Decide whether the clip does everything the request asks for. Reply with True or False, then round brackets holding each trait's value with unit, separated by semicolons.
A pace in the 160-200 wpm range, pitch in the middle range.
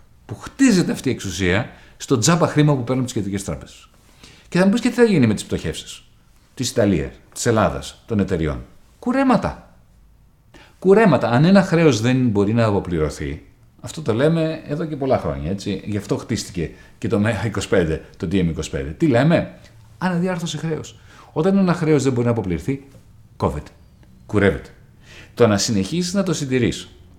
False (165 wpm; 120 Hz)